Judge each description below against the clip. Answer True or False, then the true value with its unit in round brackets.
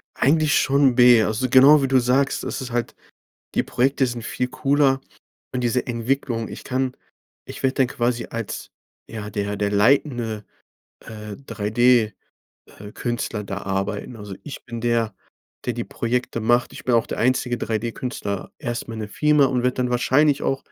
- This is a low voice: True (120 Hz)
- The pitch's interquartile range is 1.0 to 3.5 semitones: True (2.9 semitones)